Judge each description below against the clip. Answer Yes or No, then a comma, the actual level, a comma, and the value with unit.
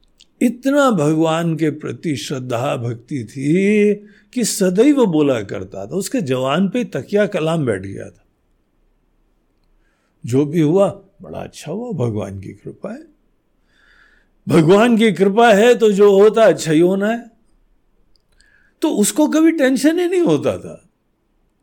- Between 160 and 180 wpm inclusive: No, average, 135 wpm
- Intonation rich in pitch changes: Yes, wide, 7.7 semitones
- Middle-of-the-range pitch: No, high, 195 Hz